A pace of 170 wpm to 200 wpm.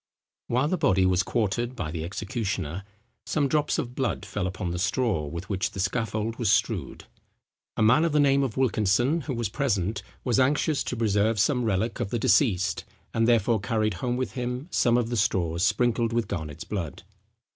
Yes: average, 190 wpm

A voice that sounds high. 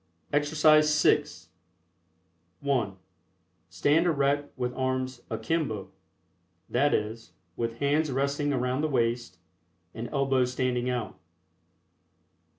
No: low, 130 Hz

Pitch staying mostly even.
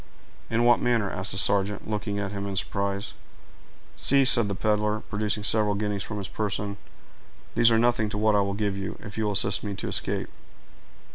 Yes: narrow, 1.4 semitones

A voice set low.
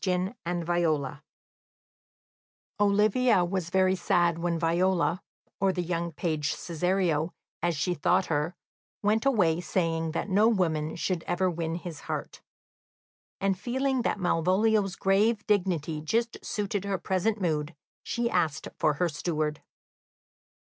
No: medium, 180 Hz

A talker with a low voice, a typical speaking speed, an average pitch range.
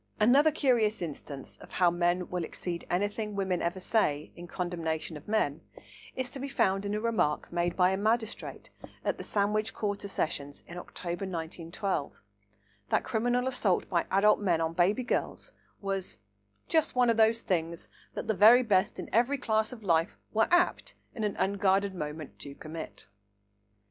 No: high, 195 Hz; average, 170 wpm; average, 4.3 semitones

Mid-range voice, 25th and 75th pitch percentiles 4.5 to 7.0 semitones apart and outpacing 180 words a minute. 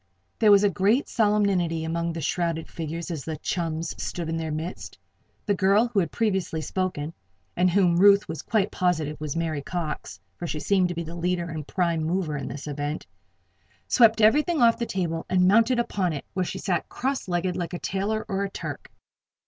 No: medium, 175 Hz; average, 3.6 semitones; average, 195 wpm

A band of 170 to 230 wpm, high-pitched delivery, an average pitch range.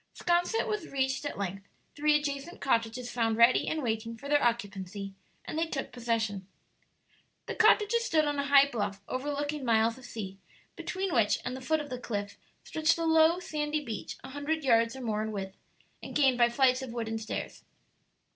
Yes: average, 185 wpm; very high, 255 Hz; average, 4.9 semitones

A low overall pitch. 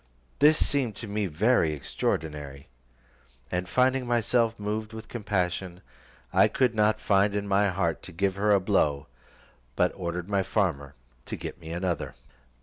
Yes: low, 100 Hz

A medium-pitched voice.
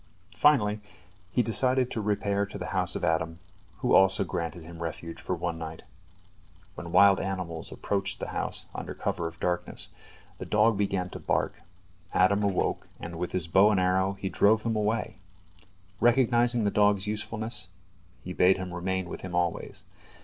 No: very low, 95 Hz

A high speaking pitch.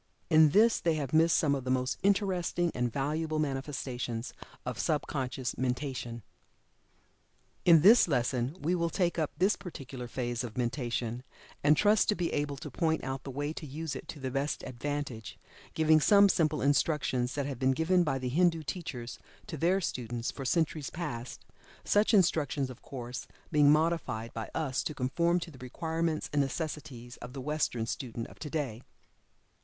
No: medium, 145 Hz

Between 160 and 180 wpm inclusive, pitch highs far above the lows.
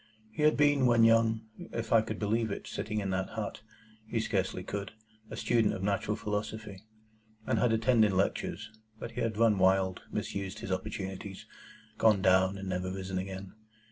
No: average, 170 wpm; average, 2.8 semitones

